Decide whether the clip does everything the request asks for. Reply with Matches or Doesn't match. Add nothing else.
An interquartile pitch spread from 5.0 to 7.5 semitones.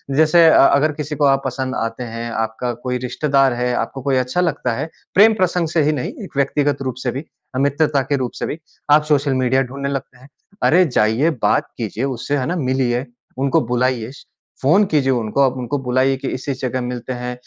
Doesn't match